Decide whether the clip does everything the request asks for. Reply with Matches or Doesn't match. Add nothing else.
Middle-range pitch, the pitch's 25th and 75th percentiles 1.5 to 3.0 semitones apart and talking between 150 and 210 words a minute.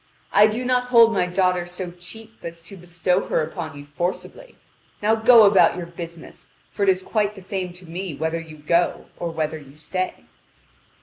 Doesn't match